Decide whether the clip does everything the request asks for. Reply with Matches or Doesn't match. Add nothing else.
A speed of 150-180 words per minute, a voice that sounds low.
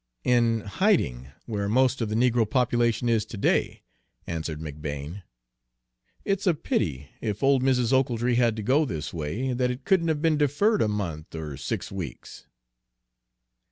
Matches